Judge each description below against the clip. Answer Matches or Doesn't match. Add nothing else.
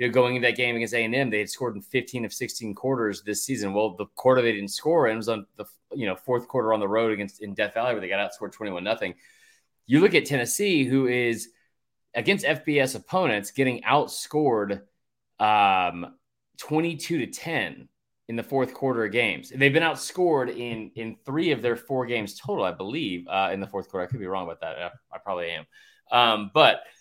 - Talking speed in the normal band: Doesn't match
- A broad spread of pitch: Doesn't match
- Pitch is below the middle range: Matches